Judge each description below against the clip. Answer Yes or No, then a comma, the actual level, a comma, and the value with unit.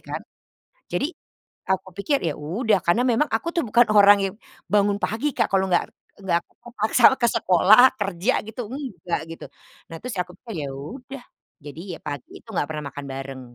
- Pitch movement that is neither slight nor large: No, wide, 5.9 semitones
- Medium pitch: No, high, 200 Hz